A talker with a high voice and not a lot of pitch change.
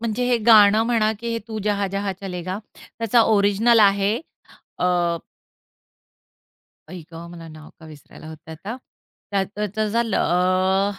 No: high, 200 Hz; average, 3.0 semitones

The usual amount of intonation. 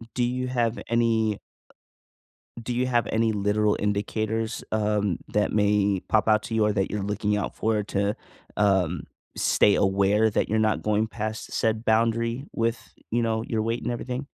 No: narrow, 1.9 semitones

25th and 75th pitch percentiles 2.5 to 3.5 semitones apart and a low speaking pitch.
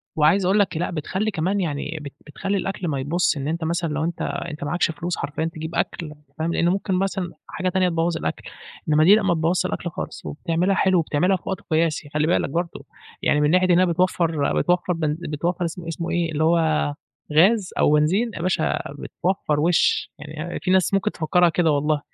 No: average, 2.8 semitones; medium, 170 Hz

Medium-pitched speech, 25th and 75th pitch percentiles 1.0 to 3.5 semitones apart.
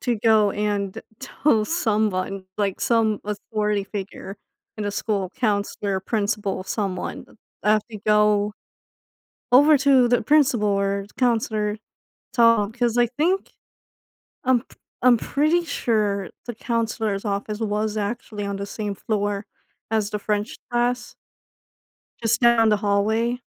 No: high, 215 Hz; average, 2.7 semitones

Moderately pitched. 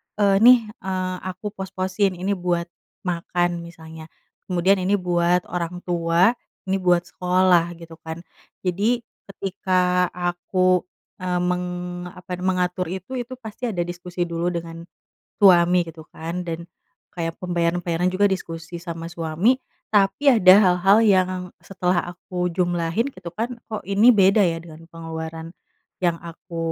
Yes: medium, 180 Hz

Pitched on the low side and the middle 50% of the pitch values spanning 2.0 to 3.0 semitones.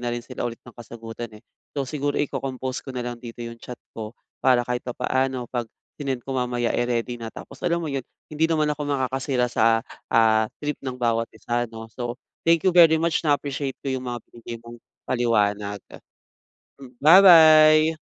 No: low, 125 Hz; average, 3.4 semitones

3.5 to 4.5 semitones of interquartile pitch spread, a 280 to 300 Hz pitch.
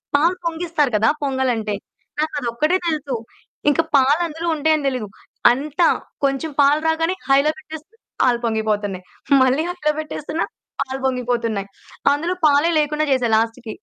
Yes: average, 4.0 semitones; very high, 285 Hz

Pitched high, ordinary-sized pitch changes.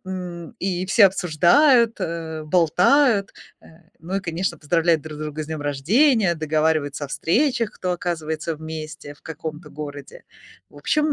No: medium, 165 Hz; average, 3.5 semitones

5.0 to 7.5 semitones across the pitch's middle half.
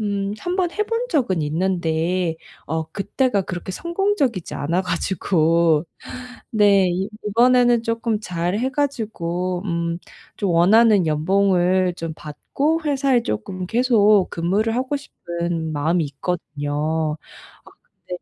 Yes: wide, 5.5 semitones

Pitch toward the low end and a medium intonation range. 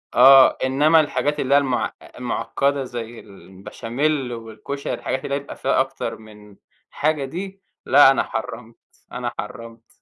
Yes: low, 130 Hz; average, 3.7 semitones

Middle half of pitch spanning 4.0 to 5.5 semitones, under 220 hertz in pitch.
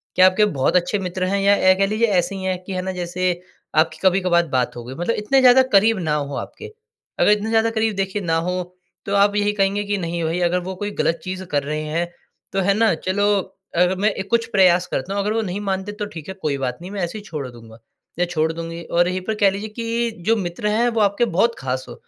No: average, 3.3 semitones; high, 190 Hz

